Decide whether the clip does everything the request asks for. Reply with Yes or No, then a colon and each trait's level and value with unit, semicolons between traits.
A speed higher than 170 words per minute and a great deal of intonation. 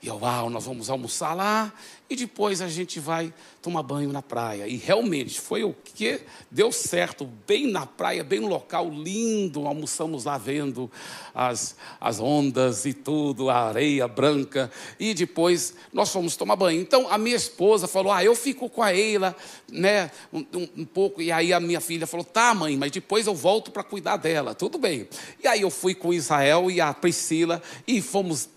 Yes: fast, 185 wpm; wide, 5.7 semitones